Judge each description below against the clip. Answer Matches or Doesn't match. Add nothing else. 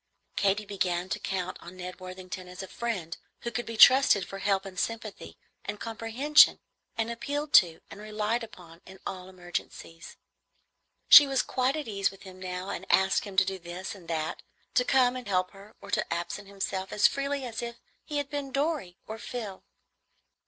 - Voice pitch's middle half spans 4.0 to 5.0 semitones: Matches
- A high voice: Matches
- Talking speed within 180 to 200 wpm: Matches